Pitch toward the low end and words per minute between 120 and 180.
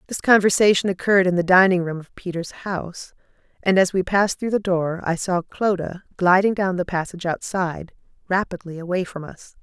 No: medium, 185 Hz; average, 170 wpm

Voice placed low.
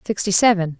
No: high, 195 Hz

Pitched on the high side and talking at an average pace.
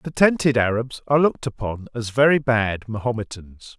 No: low, 120 Hz; average, 160 wpm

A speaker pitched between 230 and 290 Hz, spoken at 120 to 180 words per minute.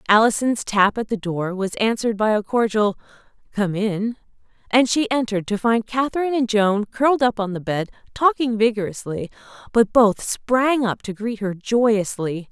No: high, 220 Hz; average, 170 wpm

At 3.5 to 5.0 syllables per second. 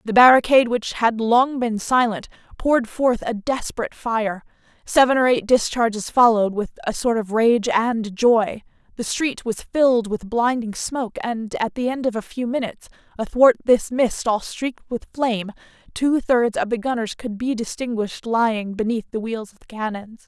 Yes: 4.9 syllables/s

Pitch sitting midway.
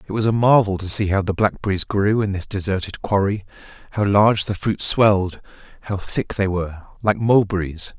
No: low, 100 Hz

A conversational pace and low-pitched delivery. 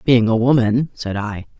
Yes: average, 190 wpm; low, 115 Hz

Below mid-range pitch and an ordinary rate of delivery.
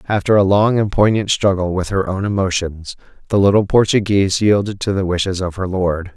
Yes: very low, 95 Hz; average, 195 wpm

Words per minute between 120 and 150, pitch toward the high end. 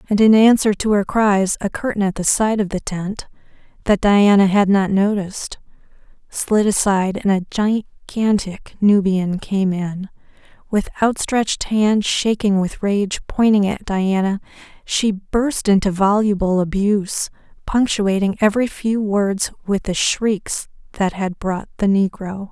Yes: average, 140 wpm; high, 200 Hz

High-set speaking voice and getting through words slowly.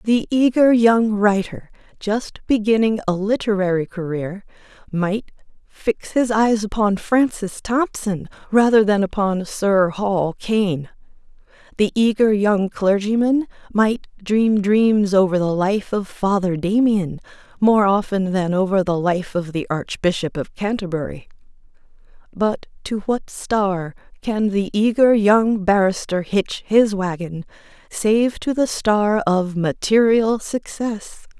Yes: high, 205 Hz; slow, 125 wpm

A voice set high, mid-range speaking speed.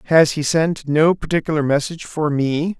No: medium, 155 Hz; average, 170 wpm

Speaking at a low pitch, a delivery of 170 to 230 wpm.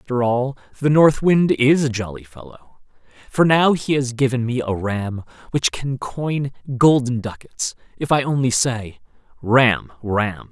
No: low, 125 Hz; average, 160 wpm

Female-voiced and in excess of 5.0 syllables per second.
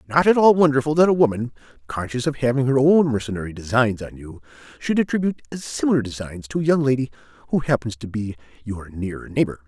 No: male; 6.2 syllables/s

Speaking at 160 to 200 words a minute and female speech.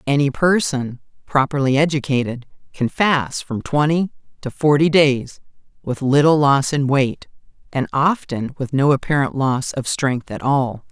No: average, 145 wpm; female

